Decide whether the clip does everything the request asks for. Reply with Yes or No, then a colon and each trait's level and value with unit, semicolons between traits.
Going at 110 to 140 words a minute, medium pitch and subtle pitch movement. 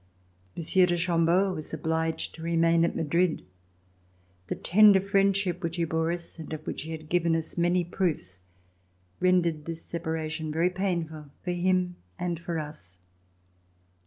No: average, 155 wpm; medium, 170 Hz; narrow, 1.9 semitones